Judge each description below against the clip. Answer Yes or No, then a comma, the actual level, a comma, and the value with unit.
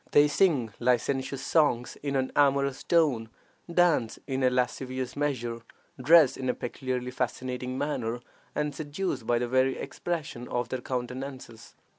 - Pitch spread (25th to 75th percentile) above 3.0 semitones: No, average, 2.7 semitones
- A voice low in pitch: Yes, low, 130 Hz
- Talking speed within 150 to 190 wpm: No, average, 140 wpm